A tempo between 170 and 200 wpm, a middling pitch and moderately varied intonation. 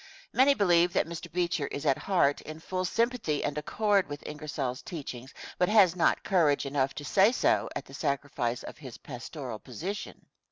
Yes: average, 175 wpm; medium, 155 Hz; average, 4.7 semitones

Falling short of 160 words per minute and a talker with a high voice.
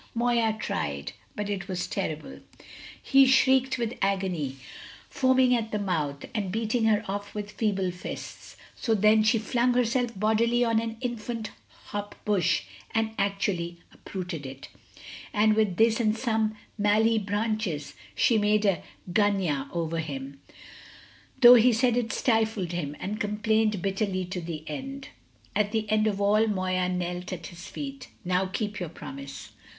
Yes: average, 150 wpm; high, 210 Hz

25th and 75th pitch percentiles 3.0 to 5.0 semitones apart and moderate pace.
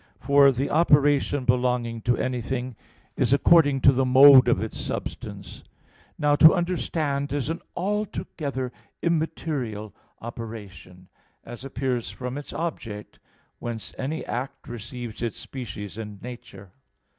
No: average, 3.6 semitones; slow, 120 wpm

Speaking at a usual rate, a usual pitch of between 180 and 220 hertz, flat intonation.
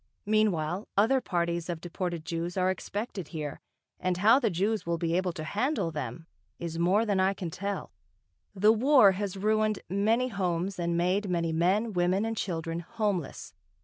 No: average, 170 wpm; medium, 185 Hz; average, 3.6 semitones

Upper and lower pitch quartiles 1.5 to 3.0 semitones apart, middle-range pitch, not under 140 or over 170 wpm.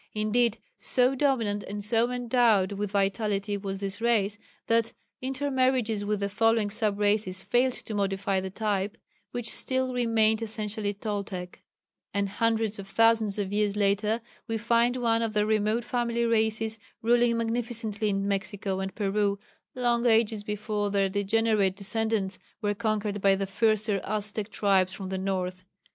No: narrow, 2.4 semitones; high, 215 Hz; average, 150 wpm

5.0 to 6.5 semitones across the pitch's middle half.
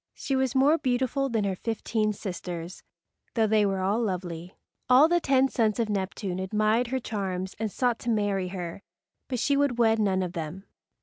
No: average, 4.6 semitones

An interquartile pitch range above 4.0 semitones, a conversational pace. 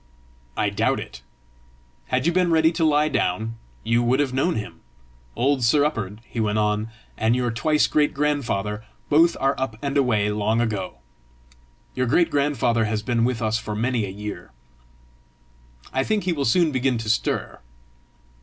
Yes: average, 5.1 semitones; average, 170 wpm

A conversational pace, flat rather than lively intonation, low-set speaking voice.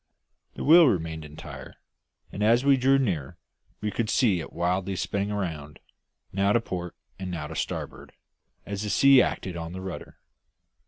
No: average, 165 wpm; average, 4.8 semitones; very low, 95 Hz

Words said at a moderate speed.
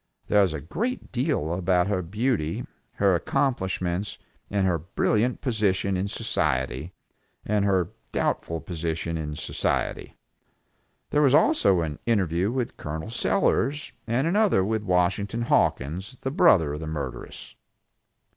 No: slow, 130 wpm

